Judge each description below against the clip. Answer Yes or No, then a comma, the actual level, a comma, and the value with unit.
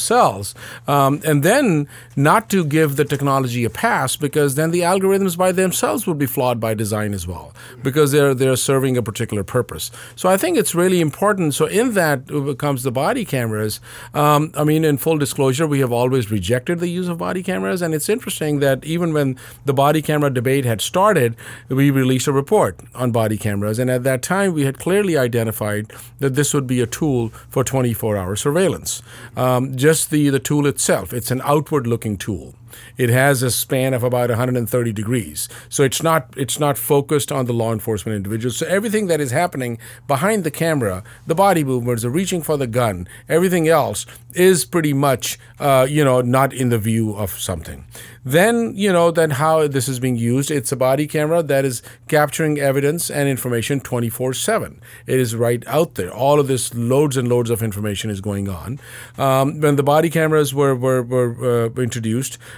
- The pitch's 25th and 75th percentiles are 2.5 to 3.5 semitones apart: No, average, 4.1 semitones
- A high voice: No, low, 135 Hz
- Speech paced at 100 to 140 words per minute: No, average, 195 wpm